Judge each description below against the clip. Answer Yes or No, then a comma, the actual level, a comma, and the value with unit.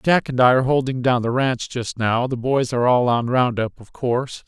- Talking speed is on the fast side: Yes, fast, 240 wpm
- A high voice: No, low, 125 Hz